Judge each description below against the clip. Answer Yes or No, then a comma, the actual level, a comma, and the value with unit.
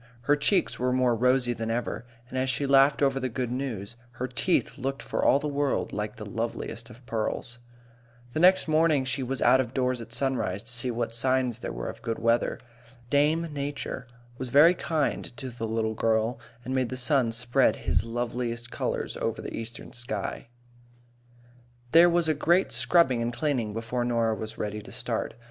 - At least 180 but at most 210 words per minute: Yes, average, 190 wpm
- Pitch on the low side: Yes, low, 125 Hz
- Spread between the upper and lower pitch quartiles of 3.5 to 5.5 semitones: No, average, 3.0 semitones